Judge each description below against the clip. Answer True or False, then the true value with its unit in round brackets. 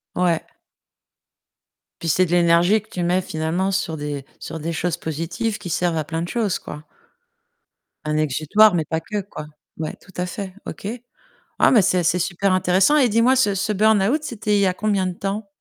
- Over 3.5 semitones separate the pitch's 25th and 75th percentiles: True (3.9 semitones)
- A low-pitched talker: False (185 Hz)